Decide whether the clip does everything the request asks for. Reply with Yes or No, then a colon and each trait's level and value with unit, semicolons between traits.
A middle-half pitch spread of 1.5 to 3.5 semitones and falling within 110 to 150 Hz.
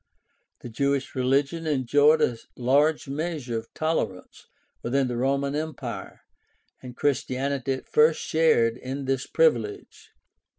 Yes: average, 3.2 semitones; medium, 140 Hz